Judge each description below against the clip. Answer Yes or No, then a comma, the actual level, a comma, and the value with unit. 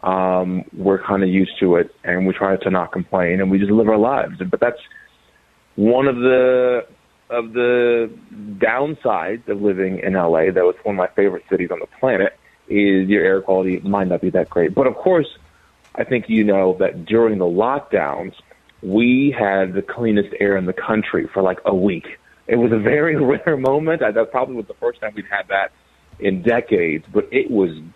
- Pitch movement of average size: Yes, average, 4.1 semitones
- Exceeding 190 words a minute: Yes, fast, 205 wpm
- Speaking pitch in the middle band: No, low, 100 Hz